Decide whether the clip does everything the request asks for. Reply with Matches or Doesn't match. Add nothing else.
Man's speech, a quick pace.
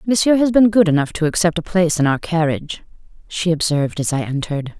Doesn't match